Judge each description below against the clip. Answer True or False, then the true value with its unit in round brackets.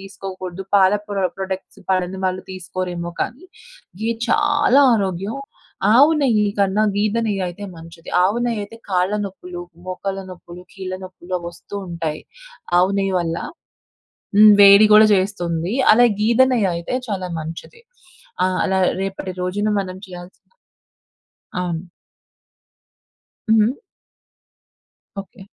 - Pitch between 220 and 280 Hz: False (190 Hz)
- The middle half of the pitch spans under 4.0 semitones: True (2.5 semitones)